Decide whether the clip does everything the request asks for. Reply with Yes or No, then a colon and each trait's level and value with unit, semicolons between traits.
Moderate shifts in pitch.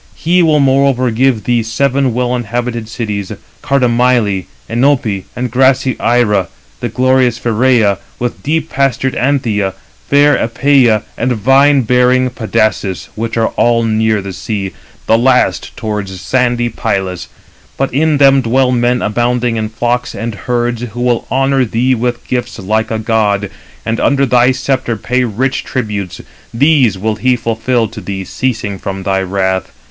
Yes: average, 3.0 semitones